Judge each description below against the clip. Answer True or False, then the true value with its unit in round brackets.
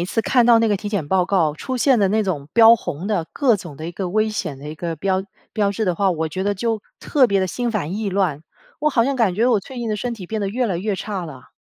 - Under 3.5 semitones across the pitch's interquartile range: False (4.3 semitones)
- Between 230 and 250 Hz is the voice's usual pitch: False (200 Hz)